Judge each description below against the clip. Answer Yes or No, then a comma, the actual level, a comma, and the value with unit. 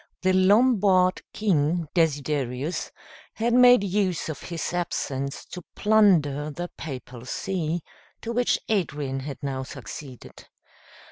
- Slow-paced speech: Yes, slow, 115 wpm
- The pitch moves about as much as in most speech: No, wide, 5.7 semitones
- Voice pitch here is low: No, medium, 170 Hz